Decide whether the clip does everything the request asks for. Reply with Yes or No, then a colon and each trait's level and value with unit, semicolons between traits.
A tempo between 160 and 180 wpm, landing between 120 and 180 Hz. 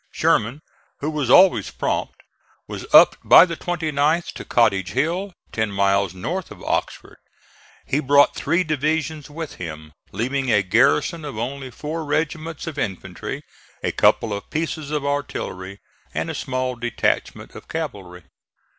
No: average, 145 wpm; medium, 140 Hz